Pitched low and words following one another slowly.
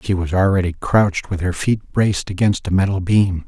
No: very low, 95 Hz; fast, 205 wpm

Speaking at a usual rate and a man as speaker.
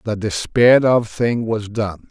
Yes: average, 170 wpm; male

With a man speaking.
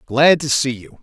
Yes: male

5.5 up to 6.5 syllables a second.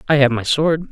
Yes: 5.8 syllables/s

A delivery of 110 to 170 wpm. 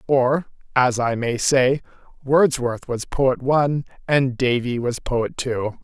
Yes: average, 145 wpm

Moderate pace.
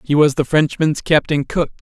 Yes: average, 190 wpm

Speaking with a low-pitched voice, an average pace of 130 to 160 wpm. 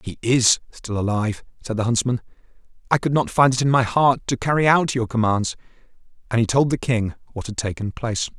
No: low, 120 Hz; fast, 205 wpm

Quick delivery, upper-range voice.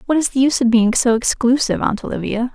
Yes: fast, 235 wpm; high, 245 Hz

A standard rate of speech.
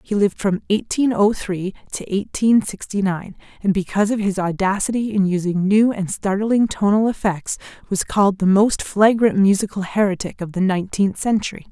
Yes: average, 170 wpm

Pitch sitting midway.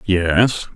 No: very low, 95 Hz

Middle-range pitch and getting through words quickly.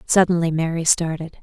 No: medium, 165 Hz; slow, 125 wpm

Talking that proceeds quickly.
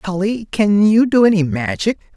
No: average, 165 wpm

